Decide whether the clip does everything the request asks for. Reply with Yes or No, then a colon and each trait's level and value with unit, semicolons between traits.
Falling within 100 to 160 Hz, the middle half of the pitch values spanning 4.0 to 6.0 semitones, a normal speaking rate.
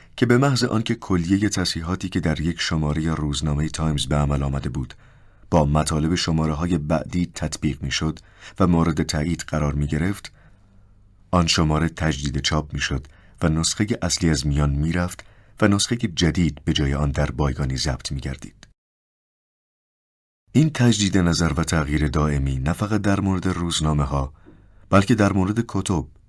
No: very low, 85 Hz; average, 4.6 semitones; average, 160 wpm